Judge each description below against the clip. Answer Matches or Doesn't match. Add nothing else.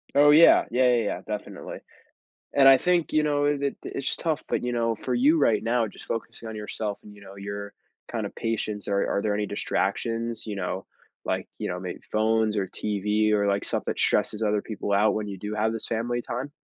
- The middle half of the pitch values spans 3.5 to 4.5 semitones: Doesn't match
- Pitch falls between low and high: Doesn't match